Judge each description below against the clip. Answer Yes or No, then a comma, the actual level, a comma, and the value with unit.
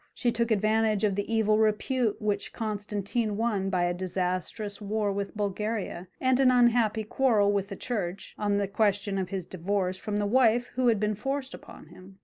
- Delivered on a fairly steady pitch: Yes, narrow, 2.3 semitones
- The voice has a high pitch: Yes, high, 210 Hz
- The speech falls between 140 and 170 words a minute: No, average, 185 wpm